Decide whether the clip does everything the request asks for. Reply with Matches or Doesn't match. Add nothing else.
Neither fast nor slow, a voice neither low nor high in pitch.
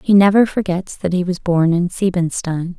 Matches